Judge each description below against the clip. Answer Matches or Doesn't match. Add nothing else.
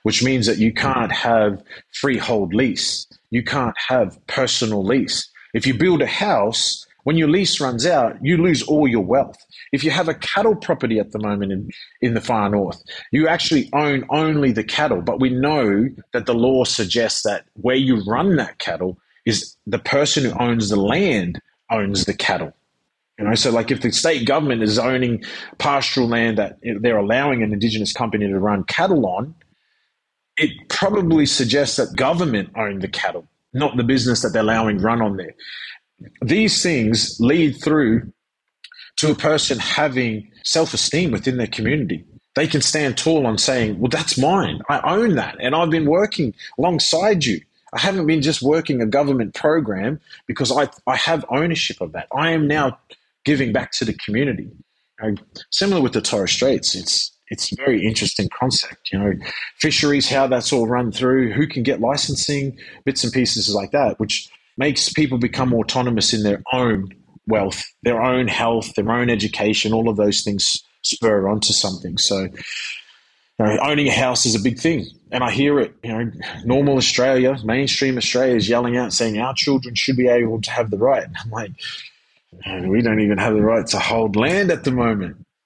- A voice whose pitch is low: Matches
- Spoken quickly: Doesn't match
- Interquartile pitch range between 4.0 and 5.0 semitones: Matches